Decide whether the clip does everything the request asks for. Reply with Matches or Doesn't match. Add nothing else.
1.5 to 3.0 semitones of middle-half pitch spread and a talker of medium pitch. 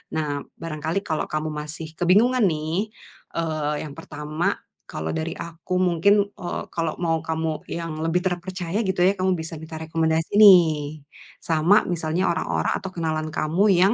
Matches